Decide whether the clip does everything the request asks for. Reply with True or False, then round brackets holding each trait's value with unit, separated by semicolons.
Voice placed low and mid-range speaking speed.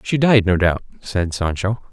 True (100 Hz; 190 wpm)